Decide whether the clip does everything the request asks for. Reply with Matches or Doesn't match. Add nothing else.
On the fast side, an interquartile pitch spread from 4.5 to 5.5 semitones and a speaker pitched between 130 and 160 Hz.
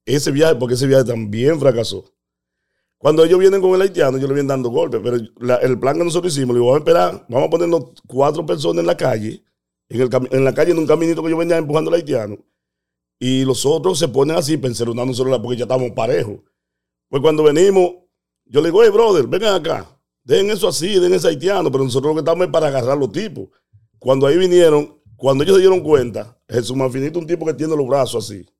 Matches